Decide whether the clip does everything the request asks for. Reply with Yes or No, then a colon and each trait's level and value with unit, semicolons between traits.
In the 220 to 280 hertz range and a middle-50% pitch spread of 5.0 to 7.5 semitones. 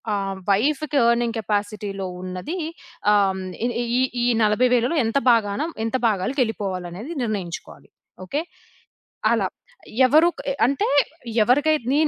Yes: high, 225 Hz; wide, 5.4 semitones